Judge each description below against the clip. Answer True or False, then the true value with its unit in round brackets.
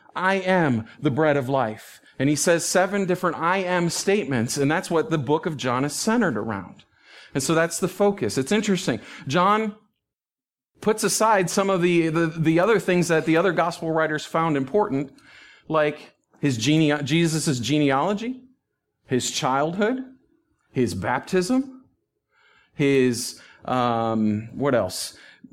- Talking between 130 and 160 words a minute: True (145 wpm)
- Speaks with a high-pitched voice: False (165 Hz)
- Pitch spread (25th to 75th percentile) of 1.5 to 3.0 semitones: False (5.3 semitones)